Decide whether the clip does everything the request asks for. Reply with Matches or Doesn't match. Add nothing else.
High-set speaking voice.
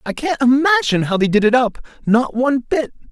Matches